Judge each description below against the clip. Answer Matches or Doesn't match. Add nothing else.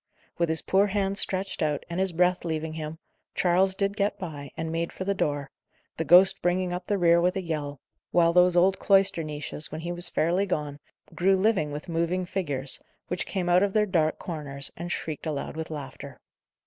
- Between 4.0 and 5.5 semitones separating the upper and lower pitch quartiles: Doesn't match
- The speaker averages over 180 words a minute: Matches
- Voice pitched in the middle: Matches